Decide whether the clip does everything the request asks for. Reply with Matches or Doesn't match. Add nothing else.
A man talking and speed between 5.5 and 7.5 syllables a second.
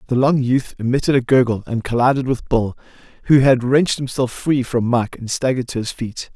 Matches